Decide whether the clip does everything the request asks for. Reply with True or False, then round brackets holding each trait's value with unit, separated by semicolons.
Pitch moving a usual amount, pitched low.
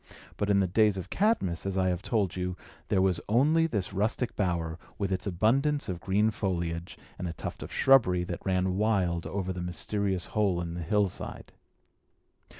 True (3.0 semitones; 95 Hz)